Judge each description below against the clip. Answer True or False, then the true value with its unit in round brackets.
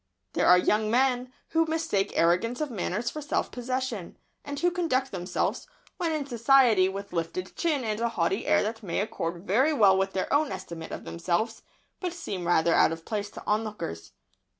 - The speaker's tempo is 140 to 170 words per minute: False (185 wpm)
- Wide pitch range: True (6.3 semitones)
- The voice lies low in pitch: False (220 Hz)